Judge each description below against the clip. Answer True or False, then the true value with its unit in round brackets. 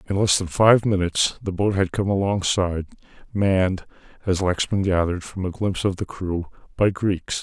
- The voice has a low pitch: True (95 Hz)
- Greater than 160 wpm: True (180 wpm)